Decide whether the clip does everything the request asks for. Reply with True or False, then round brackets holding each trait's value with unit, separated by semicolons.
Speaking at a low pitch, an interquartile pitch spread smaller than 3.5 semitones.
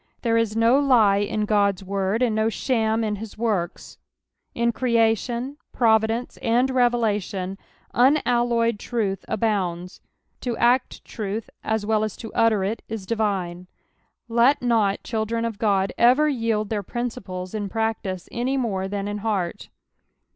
False (220 Hz; 2.7 semitones)